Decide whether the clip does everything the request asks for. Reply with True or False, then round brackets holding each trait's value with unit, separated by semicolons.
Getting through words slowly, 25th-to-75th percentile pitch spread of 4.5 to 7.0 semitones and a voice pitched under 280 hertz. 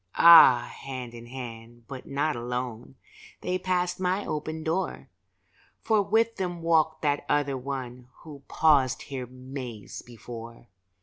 True (130 wpm; 5.0 semitones; 135 Hz)